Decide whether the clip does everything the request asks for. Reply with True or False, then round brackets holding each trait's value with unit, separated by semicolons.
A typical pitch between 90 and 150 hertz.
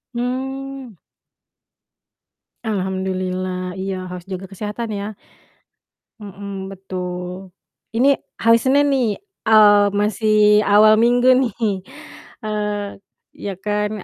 False (205 Hz)